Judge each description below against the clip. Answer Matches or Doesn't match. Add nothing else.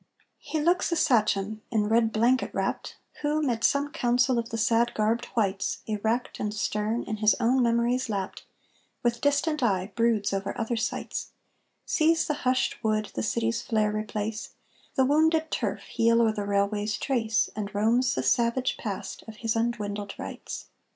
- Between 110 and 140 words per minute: Doesn't match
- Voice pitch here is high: Matches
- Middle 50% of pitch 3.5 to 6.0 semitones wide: Doesn't match